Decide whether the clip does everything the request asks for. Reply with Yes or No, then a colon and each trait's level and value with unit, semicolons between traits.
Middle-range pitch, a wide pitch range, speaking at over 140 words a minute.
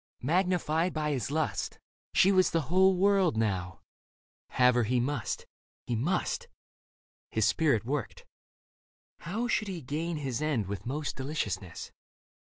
No: medium, 150 Hz; wide, 6.5 semitones; slow, 135 wpm